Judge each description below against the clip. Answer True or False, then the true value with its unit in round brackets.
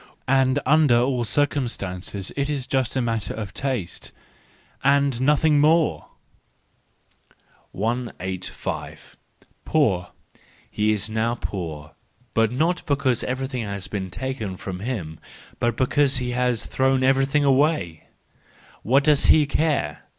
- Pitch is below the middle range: True (125 Hz)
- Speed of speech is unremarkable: False (115 wpm)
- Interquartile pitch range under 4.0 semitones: False (5.0 semitones)